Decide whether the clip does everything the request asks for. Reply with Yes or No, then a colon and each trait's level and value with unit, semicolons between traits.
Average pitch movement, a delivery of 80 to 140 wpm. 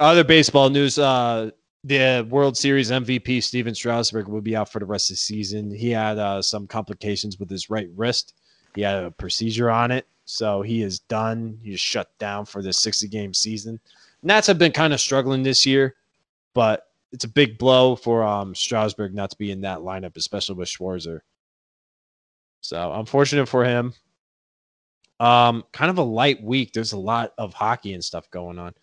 No: average, 4.0 semitones; average, 185 wpm